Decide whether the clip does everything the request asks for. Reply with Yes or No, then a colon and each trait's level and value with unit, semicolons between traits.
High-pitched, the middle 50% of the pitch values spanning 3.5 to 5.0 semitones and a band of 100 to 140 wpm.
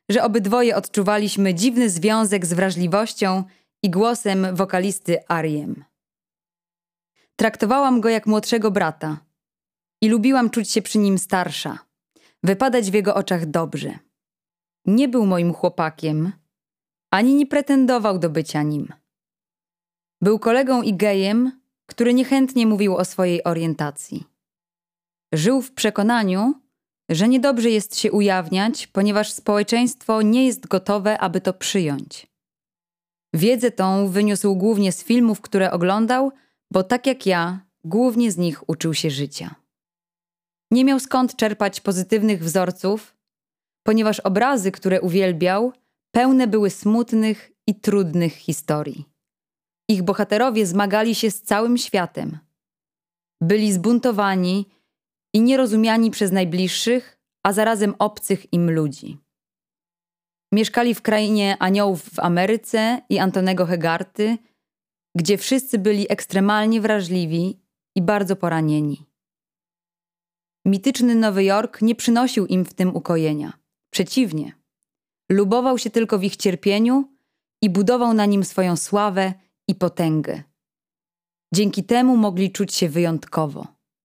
Yes: high, 200 Hz; average, 4.4 semitones; average, 115 wpm